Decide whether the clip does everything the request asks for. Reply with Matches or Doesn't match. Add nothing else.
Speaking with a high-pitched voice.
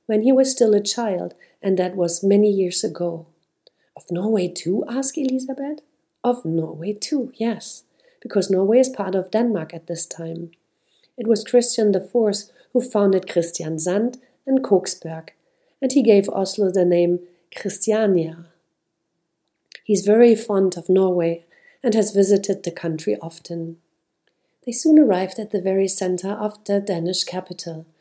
Matches